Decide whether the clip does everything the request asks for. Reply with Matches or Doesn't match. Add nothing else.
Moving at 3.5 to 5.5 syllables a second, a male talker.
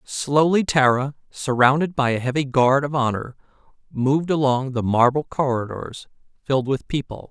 Matches